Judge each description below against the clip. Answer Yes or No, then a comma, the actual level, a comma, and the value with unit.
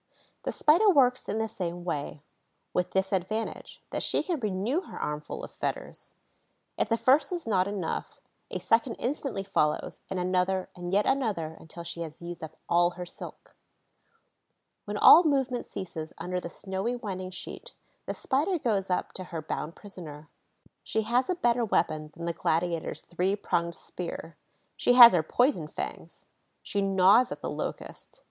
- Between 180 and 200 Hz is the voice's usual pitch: Yes, high, 190 Hz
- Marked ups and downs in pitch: Yes, wide, 5.7 semitones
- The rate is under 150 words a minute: No, average, 165 wpm